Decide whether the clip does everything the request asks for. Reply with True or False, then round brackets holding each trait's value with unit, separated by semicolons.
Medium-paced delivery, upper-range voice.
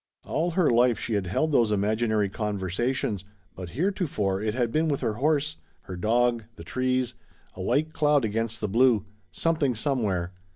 False (165 wpm; 115 Hz)